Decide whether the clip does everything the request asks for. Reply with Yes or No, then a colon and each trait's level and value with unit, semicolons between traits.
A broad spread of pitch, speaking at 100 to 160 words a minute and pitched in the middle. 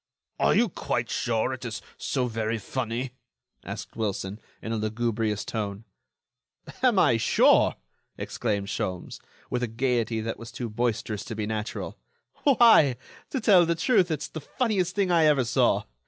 No: wide, 5.7 semitones; average, 155 wpm; low, 120 Hz